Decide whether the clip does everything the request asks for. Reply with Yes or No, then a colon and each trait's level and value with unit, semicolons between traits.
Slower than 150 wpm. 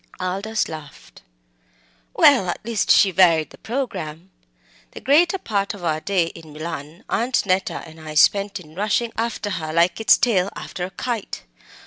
No: average, 160 wpm